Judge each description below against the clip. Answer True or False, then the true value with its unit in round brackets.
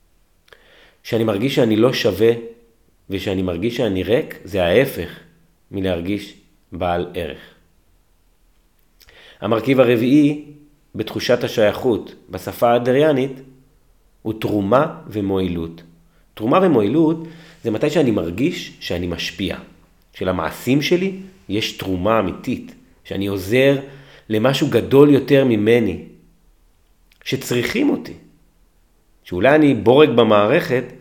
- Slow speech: True (95 wpm)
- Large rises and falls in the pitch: True (6.4 semitones)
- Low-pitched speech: True (110 Hz)